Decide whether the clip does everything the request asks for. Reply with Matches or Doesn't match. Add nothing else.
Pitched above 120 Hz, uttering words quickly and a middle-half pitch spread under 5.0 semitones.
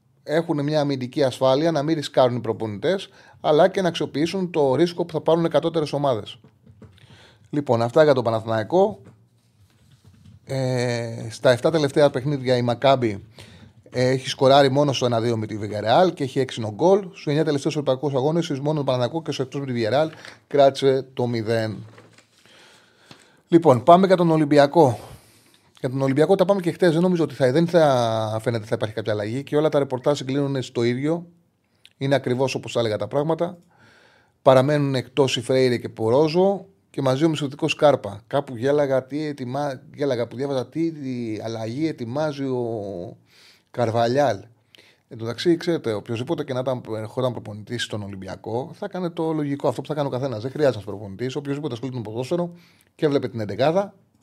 Matches